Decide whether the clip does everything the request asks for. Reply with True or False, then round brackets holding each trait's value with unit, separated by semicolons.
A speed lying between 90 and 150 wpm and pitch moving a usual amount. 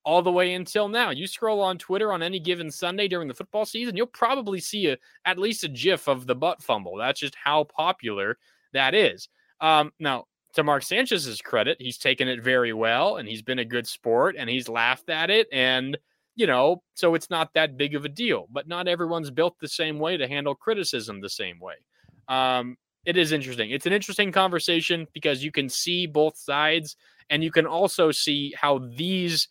False (205 wpm; 4.7 semitones)